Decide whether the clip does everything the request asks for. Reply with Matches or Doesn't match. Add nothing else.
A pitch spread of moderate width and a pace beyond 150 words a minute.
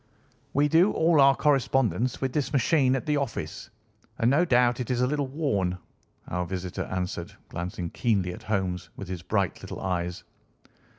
Doesn't match